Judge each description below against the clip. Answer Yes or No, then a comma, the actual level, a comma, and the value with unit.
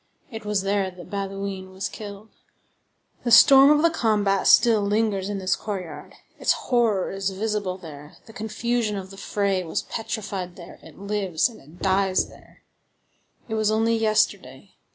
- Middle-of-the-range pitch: No, high, 200 Hz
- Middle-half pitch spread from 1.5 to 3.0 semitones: Yes, narrow, 2.6 semitones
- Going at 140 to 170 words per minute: Yes, average, 160 wpm